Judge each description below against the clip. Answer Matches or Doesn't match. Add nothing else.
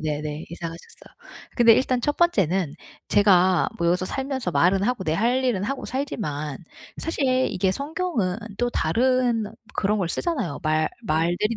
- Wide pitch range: Matches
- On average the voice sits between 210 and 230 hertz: Doesn't match